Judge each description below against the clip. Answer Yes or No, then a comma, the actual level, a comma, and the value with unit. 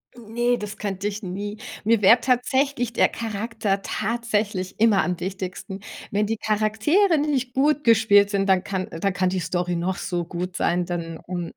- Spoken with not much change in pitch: No, average, 3.8 semitones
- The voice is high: Yes, high, 205 Hz